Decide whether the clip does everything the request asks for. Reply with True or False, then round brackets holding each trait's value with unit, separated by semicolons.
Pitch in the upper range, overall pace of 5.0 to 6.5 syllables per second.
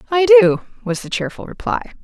True (235 Hz; 5.2 syllables/s)